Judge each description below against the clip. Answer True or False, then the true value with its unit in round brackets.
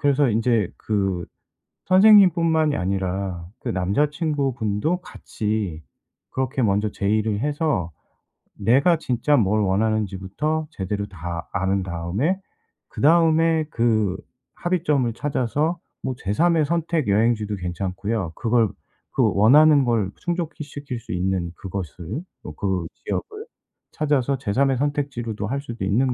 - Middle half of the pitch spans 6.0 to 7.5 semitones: True (7.2 semitones)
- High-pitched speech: False (115 Hz)